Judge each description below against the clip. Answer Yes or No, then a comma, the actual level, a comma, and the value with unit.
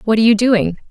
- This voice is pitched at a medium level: No, high, 220 Hz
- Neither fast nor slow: No, fast, 265 wpm